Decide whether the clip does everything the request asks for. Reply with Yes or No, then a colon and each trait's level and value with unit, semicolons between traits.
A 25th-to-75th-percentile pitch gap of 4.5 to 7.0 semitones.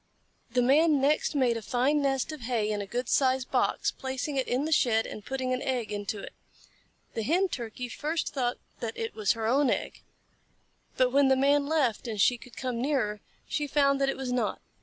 No: average, 3.1 semitones